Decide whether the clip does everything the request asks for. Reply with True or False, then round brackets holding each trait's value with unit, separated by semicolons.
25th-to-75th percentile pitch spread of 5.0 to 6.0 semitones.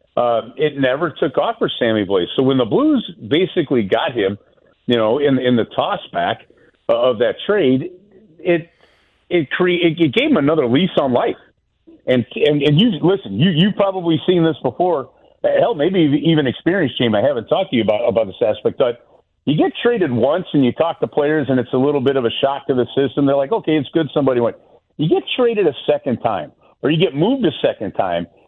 True (5.4 semitones)